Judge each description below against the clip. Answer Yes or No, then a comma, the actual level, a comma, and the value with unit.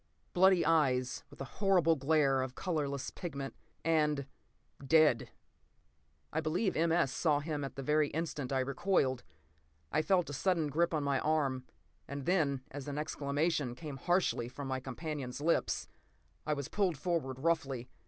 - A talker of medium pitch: Yes, medium, 150 Hz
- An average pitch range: Yes, average, 3.3 semitones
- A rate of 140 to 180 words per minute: Yes, average, 155 wpm